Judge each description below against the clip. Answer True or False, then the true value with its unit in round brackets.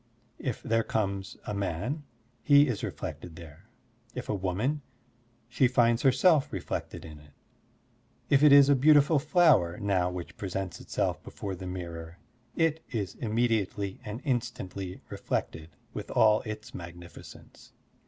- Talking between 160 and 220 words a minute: False (135 wpm)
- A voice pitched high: False (105 Hz)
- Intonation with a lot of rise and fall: True (6.4 semitones)